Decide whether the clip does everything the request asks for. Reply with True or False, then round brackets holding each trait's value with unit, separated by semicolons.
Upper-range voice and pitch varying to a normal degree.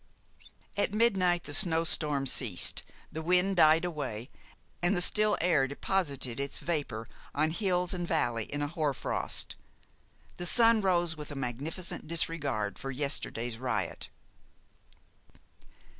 False (155 Hz; 4.7 semitones)